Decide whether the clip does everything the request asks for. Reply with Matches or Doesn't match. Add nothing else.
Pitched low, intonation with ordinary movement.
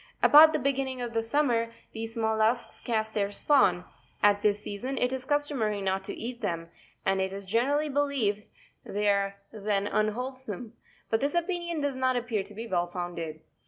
Doesn't match